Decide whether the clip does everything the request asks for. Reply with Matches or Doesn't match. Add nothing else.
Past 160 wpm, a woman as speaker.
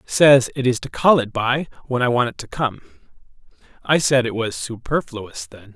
Doesn't match